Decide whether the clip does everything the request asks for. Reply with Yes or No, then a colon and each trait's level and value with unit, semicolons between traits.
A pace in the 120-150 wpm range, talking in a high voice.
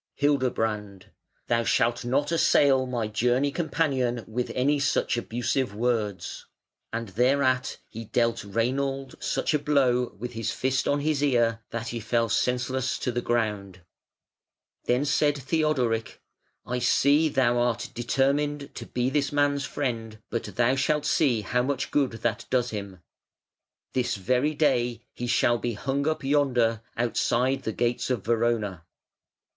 No: average, 145 wpm; low, 125 Hz